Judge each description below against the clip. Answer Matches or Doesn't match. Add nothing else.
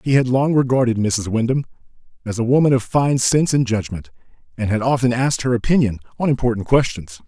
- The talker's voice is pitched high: Doesn't match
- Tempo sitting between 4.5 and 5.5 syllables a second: Doesn't match